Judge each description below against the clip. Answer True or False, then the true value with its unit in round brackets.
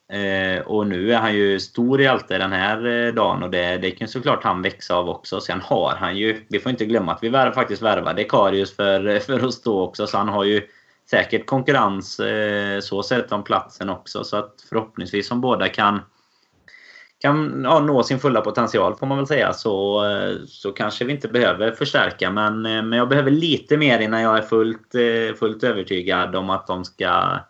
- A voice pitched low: True (110 Hz)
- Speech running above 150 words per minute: True (195 wpm)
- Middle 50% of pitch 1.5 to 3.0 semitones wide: False (3.6 semitones)